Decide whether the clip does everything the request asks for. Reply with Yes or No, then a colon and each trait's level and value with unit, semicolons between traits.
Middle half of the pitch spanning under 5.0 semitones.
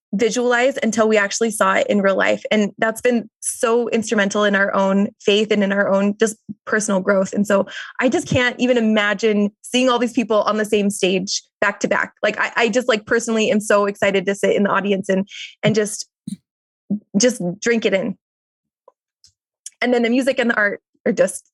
Yes: average, 2.7 semitones